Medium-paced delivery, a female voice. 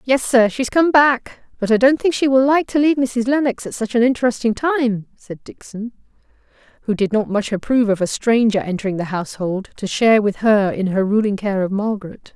No: fast, 215 wpm; female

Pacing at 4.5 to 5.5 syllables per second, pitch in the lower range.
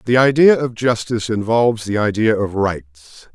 Yes: 4.8 syllables/s; low, 110 Hz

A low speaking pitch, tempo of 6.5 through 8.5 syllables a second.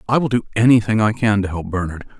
Yes: low, 105 Hz; 6.6 syllables/s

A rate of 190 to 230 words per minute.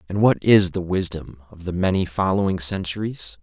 No: average, 175 wpm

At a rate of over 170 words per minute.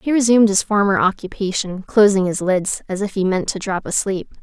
Yes: fast, 205 wpm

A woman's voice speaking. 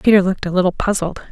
Yes: female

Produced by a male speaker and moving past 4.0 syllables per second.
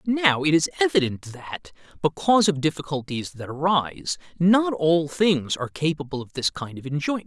Yes: male; 5.2 syllables/s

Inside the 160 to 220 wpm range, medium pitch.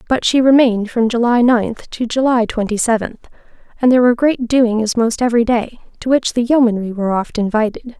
No: average, 190 wpm; high, 235 Hz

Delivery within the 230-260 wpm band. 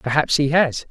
No: average, 200 wpm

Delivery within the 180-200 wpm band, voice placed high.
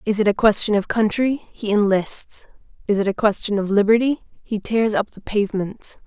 Yes: average, 190 wpm; high, 210 Hz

